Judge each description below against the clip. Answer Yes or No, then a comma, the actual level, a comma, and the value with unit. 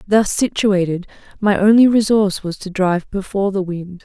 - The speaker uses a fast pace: No, average, 165 wpm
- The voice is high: Yes, high, 195 Hz